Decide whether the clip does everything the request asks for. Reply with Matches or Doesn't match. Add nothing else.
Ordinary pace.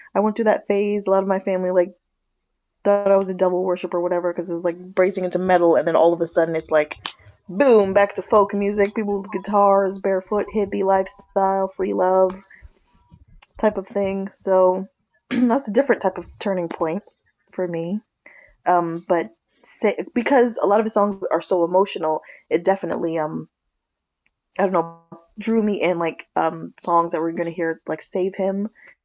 Matches